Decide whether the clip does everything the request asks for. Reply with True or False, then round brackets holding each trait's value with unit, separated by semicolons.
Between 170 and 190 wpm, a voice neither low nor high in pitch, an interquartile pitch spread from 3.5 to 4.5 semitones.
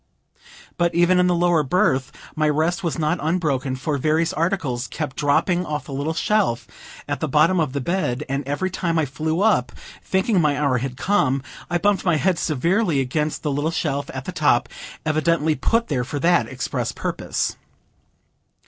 True (180 wpm; 155 Hz; 3.9 semitones)